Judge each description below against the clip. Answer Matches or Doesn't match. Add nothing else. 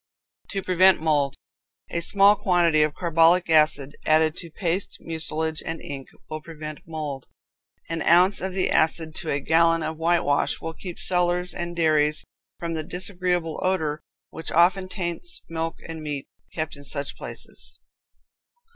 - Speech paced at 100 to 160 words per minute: Matches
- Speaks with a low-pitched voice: Doesn't match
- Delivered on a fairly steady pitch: Matches